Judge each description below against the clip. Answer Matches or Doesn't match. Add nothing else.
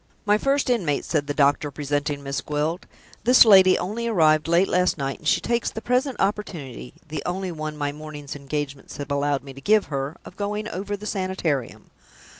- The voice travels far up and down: Matches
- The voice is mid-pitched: Matches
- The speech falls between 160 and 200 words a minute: Matches